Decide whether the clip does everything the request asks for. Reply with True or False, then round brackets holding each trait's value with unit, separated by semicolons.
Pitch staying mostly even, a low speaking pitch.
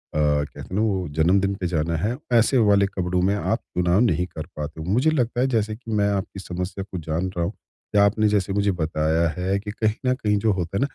False (3.5 semitones; 95 Hz)